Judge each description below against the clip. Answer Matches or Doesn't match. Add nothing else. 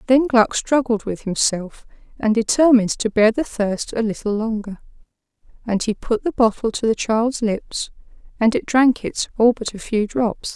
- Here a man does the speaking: Doesn't match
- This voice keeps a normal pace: Matches